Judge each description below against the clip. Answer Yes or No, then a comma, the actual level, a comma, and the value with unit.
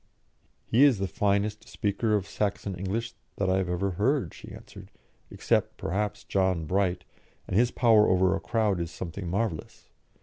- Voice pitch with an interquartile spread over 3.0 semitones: No, narrow, 2.6 semitones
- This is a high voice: No, low, 100 Hz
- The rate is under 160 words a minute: No, average, 165 wpm